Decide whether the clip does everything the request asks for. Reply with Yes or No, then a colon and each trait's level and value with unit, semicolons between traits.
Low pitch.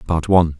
Yes: very low, 80 Hz